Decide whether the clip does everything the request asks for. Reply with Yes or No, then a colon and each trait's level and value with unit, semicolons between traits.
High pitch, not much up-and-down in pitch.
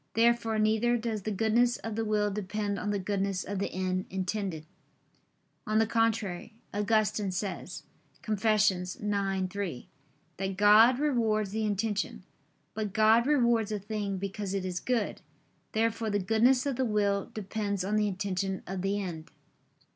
Yes: high, 210 Hz; narrow, 2.3 semitones